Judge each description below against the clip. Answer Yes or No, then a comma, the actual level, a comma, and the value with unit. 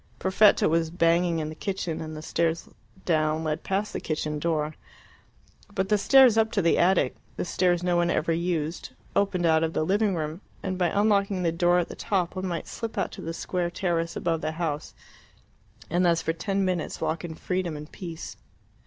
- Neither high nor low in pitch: Yes, medium, 170 Hz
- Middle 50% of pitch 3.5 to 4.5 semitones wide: No, average, 2.7 semitones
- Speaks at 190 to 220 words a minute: Yes, average, 200 wpm